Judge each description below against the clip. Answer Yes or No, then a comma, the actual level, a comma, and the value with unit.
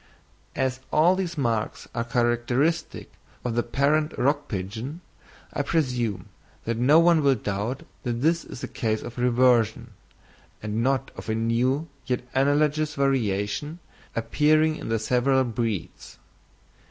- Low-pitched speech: Yes, low, 125 Hz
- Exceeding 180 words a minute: No, slow, 135 wpm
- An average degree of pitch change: Yes, average, 4.1 semitones